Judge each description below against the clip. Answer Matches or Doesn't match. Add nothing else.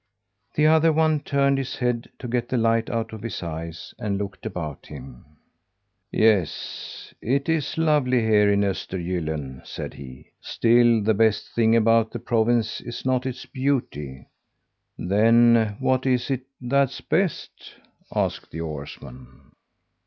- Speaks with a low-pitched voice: Matches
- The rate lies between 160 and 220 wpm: Doesn't match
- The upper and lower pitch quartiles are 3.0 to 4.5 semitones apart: Doesn't match